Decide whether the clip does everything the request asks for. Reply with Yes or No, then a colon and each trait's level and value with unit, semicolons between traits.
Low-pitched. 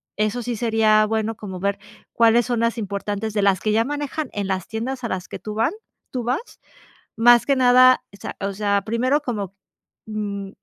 No: high, 220 Hz